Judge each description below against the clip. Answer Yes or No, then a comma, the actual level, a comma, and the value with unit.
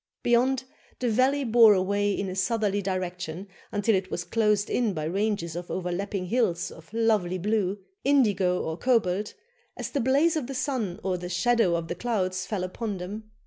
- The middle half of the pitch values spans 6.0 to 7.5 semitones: No, average, 4.1 semitones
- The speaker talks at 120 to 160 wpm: No, average, 180 wpm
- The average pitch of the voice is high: Yes, high, 205 Hz